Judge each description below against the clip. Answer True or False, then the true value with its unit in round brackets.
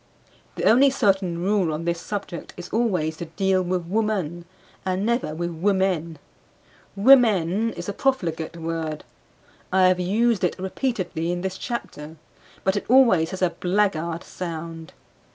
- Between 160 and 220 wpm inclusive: False (145 wpm)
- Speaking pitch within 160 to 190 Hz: True (185 Hz)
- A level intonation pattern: False (3.5 semitones)